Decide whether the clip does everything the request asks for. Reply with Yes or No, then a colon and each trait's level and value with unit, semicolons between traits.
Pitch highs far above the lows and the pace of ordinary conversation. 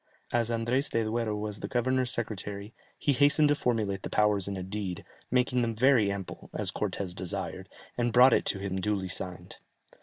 No: average, 3.7 semitones; average, 185 wpm